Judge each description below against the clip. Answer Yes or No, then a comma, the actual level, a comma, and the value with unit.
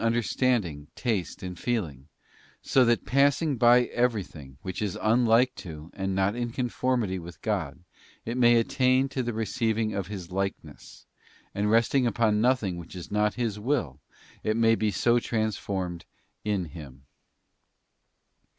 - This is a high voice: No, low, 110 Hz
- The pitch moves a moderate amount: Yes, average, 4.5 semitones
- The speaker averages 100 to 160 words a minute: Yes, average, 150 wpm